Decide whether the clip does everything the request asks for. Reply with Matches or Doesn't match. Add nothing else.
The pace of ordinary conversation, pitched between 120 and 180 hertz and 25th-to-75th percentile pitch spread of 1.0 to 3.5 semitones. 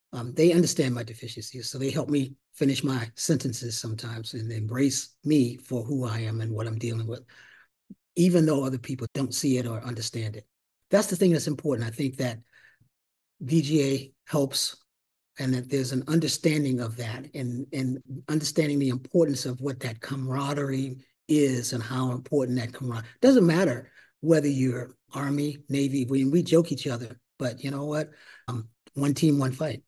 Matches